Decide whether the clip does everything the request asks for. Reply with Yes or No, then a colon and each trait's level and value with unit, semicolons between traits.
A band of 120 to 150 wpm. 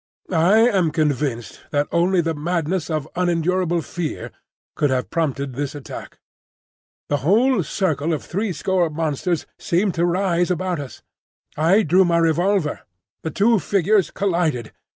Yes: slow, 135 wpm